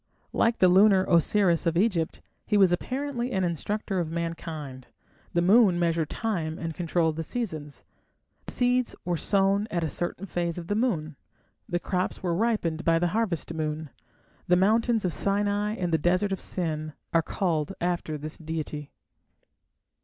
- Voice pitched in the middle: Yes, medium, 175 Hz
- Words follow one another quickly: No, average, 160 wpm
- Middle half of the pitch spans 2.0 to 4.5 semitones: Yes, average, 3.9 semitones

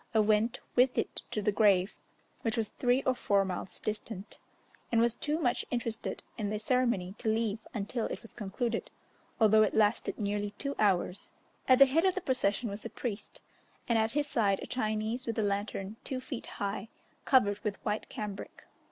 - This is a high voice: Yes, high, 220 Hz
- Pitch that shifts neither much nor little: Yes, average, 3.1 semitones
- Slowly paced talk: No, average, 185 wpm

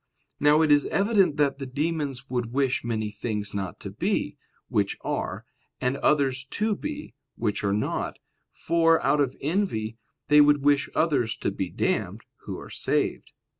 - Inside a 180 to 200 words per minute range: No, average, 165 wpm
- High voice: No, medium, 140 Hz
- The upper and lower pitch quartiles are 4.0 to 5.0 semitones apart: Yes, average, 4.6 semitones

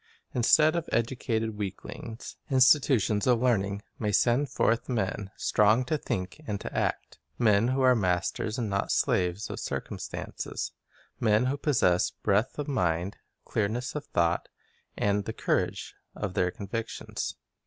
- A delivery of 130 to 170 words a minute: Yes, average, 145 wpm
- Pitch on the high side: No, low, 110 Hz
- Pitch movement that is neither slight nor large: Yes, average, 4.2 semitones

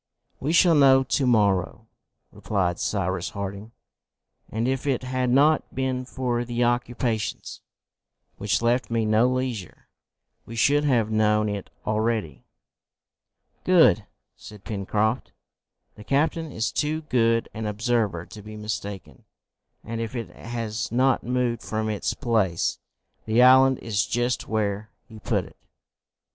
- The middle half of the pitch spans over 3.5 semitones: No, average, 3.1 semitones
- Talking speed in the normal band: No, slow, 130 wpm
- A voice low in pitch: Yes, low, 115 Hz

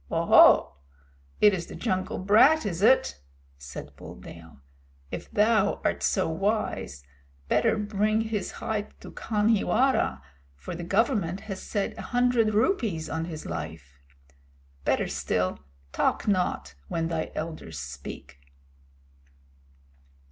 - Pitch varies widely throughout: Yes, wide, 5.7 semitones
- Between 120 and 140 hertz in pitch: No, high, 195 Hz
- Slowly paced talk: Yes, slow, 120 wpm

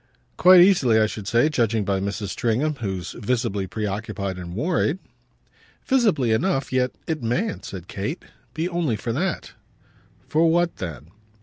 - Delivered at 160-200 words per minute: No, average, 145 wpm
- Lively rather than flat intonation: Yes, wide, 8.1 semitones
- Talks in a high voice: No, low, 115 Hz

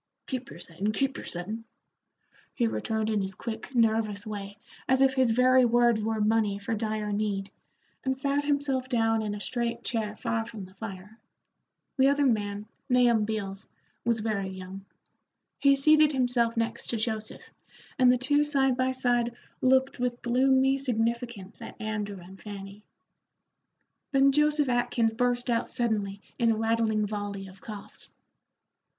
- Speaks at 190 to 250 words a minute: No, average, 155 wpm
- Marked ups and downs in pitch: No, average, 3.5 semitones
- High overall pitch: Yes, high, 230 Hz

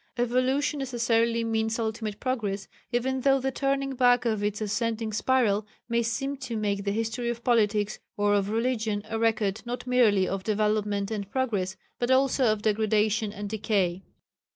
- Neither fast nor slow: Yes, average, 160 wpm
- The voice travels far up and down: No, average, 2.9 semitones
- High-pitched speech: Yes, high, 225 Hz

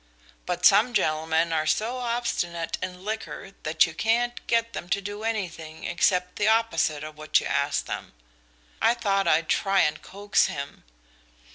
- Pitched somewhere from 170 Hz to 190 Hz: Yes, medium, 185 Hz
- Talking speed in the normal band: Yes, average, 160 wpm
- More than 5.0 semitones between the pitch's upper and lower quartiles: Yes, wide, 5.5 semitones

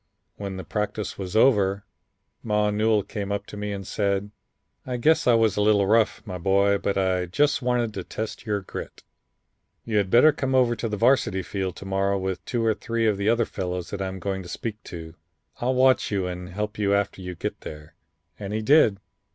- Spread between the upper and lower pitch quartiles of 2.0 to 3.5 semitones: Yes, average, 2.7 semitones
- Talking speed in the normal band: No, fast, 215 wpm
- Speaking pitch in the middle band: No, low, 100 Hz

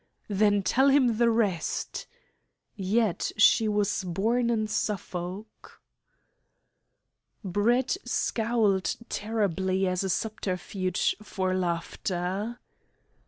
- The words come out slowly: Yes, slow, 85 wpm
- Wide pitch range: No, average, 3.2 semitones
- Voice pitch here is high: Yes, high, 205 Hz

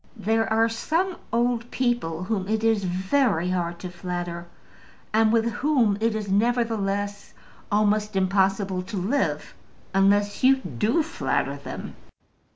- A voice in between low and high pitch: No, high, 210 Hz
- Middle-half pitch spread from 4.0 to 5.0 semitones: No, average, 3.4 semitones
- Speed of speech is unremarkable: No, slow, 130 wpm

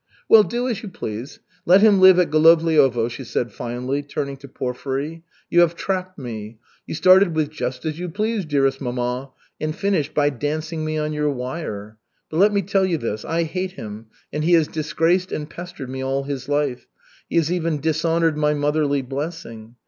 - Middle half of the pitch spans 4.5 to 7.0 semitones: No, average, 4.1 semitones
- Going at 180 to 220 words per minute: Yes, average, 190 wpm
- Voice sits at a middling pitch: Yes, medium, 150 Hz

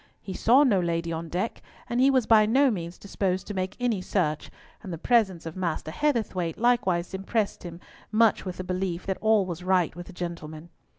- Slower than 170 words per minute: No, average, 200 wpm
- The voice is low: No, medium, 185 Hz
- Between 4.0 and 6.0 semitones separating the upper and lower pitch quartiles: Yes, average, 4.3 semitones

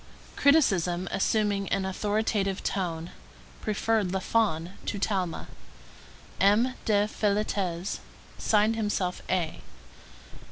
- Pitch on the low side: No, high, 200 Hz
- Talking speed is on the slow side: Yes, slow, 85 wpm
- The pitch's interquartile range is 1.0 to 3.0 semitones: Yes, narrow, 2.6 semitones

